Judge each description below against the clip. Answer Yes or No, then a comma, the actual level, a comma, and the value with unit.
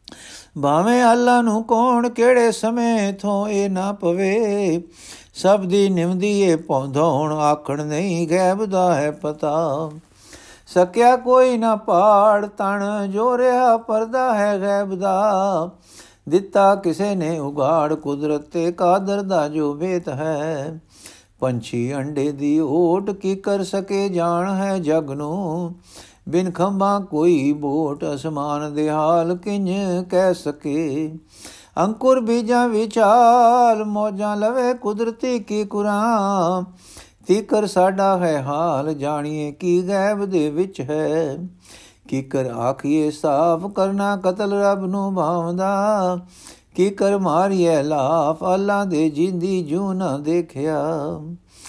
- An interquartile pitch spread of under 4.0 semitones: No, average, 4.5 semitones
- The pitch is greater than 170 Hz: Yes, medium, 185 Hz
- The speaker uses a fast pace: No, average, 115 wpm